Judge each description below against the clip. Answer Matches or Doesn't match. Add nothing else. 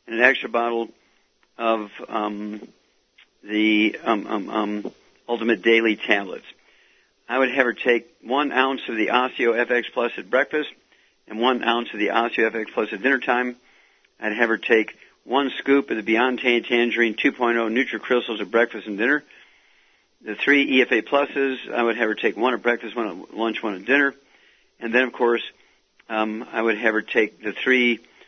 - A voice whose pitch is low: Matches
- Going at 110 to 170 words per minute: Doesn't match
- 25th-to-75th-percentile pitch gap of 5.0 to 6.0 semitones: Doesn't match